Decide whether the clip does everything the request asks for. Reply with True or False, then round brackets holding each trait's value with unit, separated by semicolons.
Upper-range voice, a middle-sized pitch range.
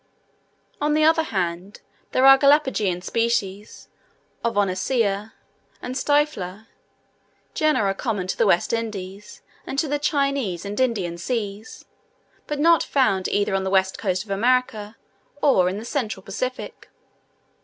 False (215 Hz; 5.7 semitones)